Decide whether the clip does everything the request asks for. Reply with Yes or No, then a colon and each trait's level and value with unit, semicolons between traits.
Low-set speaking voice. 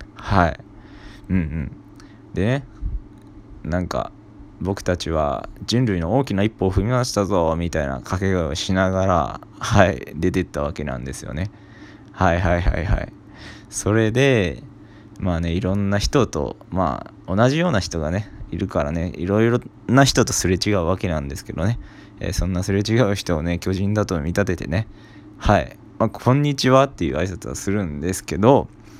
Yes: low, 100 Hz